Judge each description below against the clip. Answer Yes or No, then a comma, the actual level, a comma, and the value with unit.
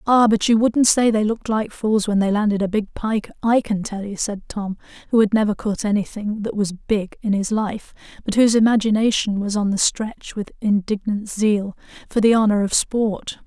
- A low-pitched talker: No, high, 210 Hz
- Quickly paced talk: Yes, fast, 210 wpm